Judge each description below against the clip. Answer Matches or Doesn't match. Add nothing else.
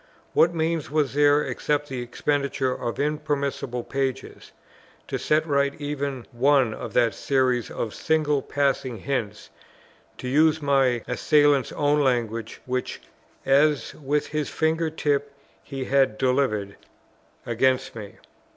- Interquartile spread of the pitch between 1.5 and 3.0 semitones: Matches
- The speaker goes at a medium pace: Doesn't match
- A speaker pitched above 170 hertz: Doesn't match